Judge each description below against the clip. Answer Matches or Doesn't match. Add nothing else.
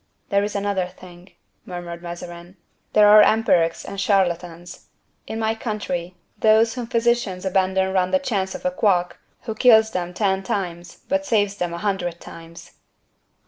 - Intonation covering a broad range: Doesn't match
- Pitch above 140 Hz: Matches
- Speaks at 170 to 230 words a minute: Doesn't match